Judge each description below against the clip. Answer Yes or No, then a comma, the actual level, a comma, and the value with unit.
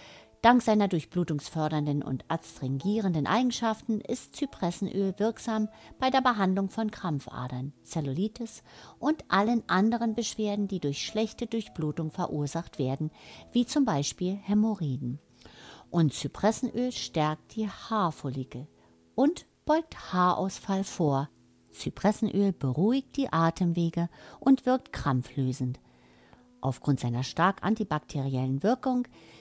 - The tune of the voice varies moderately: No, wide, 7.8 semitones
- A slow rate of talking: Yes, slow, 100 wpm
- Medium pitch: Yes, medium, 180 Hz